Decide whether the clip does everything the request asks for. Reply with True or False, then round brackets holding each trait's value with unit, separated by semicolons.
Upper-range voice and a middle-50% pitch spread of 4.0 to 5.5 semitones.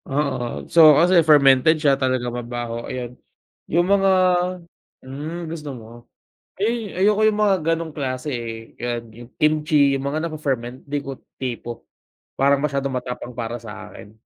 False (140 Hz; 4.5 semitones)